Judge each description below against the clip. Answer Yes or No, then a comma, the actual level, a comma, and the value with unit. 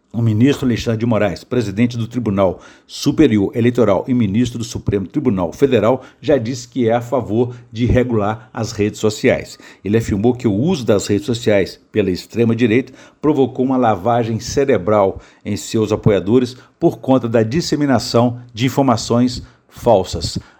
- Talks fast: No, average, 150 wpm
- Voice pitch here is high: No, low, 120 Hz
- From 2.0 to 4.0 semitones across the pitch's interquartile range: Yes, average, 2.8 semitones